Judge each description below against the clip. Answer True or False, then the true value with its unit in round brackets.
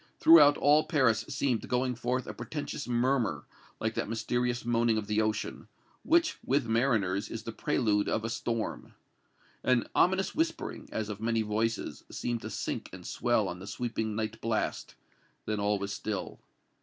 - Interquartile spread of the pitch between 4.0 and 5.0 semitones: False (3.0 semitones)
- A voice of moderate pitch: False (115 Hz)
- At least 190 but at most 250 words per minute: False (165 wpm)